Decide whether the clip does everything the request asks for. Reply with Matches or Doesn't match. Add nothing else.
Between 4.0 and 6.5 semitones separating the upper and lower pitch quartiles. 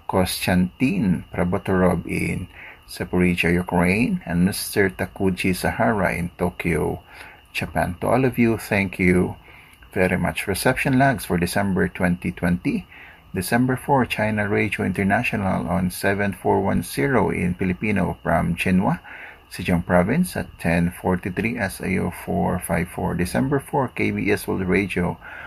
Doesn't match